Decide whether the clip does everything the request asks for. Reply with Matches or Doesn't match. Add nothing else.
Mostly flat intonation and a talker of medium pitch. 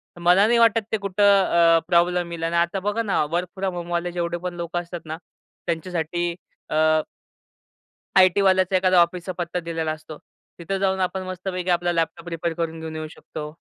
Matches